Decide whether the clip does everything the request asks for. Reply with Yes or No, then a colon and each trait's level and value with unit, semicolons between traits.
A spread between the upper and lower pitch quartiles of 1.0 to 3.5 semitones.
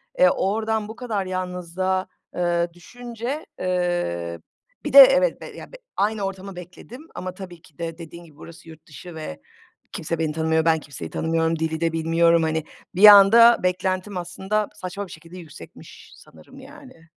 No: average, 4.0 semitones